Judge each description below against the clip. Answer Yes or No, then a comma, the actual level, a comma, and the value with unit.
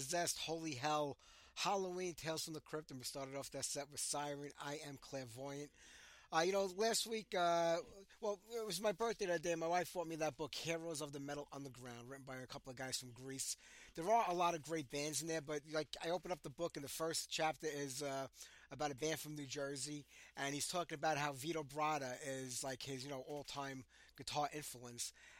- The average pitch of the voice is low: No, medium, 150 Hz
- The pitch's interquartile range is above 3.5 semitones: No, average, 3.2 semitones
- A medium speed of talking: No, fast, 225 wpm